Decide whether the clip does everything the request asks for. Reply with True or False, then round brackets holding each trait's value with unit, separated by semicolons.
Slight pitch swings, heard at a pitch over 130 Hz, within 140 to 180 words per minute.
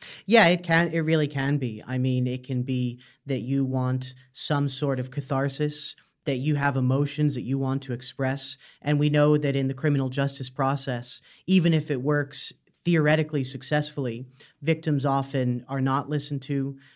True (2.1 semitones; 140 Hz; 175 wpm)